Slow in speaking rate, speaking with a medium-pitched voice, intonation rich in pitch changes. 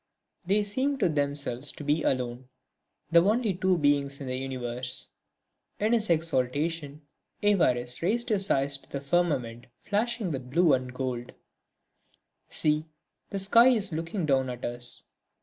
No: average, 145 wpm; medium, 150 Hz; wide, 6.9 semitones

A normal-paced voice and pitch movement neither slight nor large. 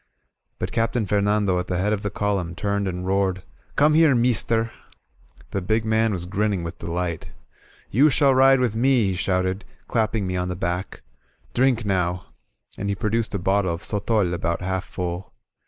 Yes: average, 180 wpm; average, 3.7 semitones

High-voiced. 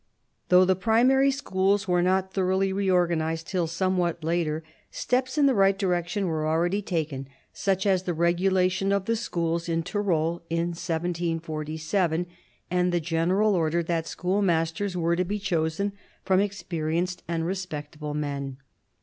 No: medium, 175 Hz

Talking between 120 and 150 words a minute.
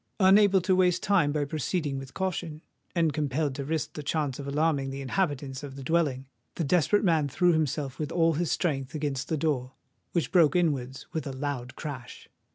No: average, 190 wpm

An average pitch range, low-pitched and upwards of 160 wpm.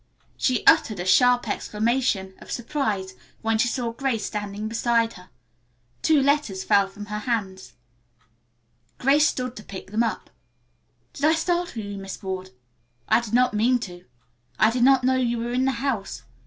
No: average, 4.1 semitones; high, 230 Hz; average, 170 wpm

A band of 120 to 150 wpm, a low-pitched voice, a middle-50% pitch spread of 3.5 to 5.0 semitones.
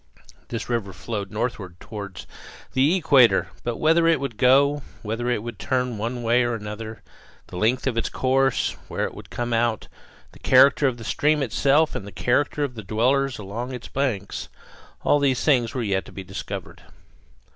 No: average, 180 wpm; low, 120 Hz; average, 3.8 semitones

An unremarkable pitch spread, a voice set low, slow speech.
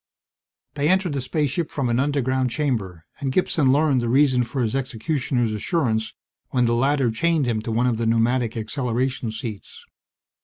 No: average, 3.6 semitones; low, 125 Hz; average, 165 wpm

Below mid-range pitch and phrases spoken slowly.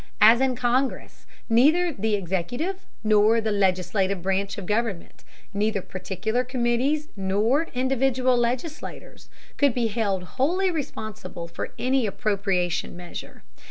No: high, 225 Hz; slow, 115 wpm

